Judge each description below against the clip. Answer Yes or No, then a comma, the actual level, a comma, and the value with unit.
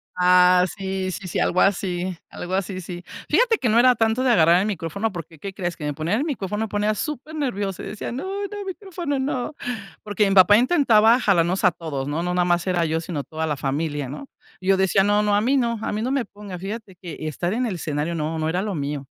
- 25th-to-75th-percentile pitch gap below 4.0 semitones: No, average, 4.9 semitones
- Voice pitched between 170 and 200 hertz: Yes, high, 190 Hz